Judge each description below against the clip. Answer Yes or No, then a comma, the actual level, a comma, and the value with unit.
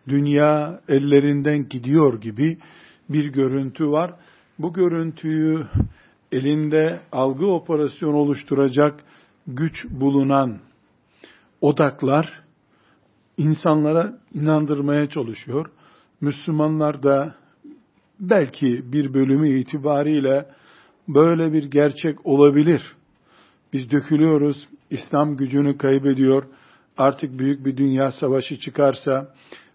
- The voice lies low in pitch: No, medium, 145 Hz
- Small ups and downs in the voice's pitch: Yes, narrow, 2.1 semitones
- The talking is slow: Yes, slow, 80 wpm